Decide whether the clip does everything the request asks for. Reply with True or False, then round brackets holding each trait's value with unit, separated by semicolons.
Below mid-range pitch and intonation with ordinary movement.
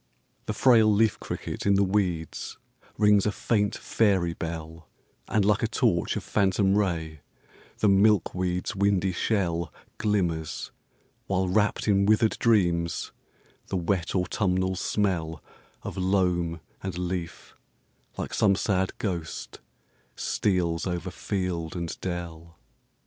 True (95 Hz; 3.1 semitones)